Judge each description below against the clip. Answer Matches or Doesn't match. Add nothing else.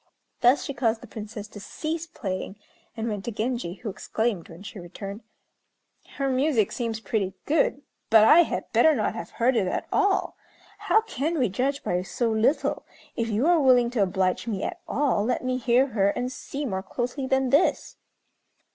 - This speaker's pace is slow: Doesn't match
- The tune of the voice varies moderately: Matches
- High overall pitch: Matches